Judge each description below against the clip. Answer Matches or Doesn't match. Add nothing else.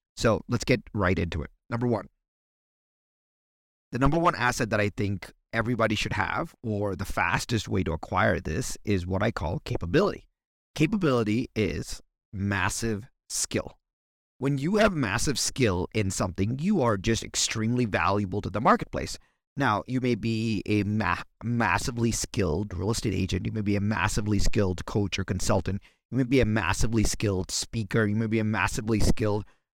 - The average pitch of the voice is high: Doesn't match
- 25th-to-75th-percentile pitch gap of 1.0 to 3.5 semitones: Matches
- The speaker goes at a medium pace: Matches